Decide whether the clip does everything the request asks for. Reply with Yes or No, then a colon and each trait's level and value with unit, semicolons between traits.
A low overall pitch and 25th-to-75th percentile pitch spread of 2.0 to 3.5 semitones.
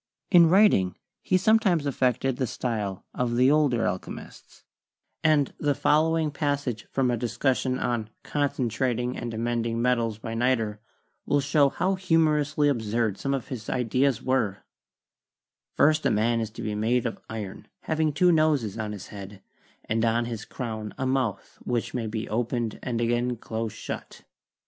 No: low, 125 Hz; average, 4.2 semitones